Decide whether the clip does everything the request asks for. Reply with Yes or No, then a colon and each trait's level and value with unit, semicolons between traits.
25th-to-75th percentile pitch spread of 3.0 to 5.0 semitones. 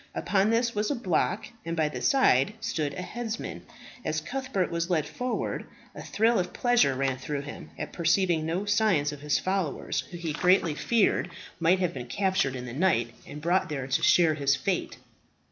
No: wide, 5.4 semitones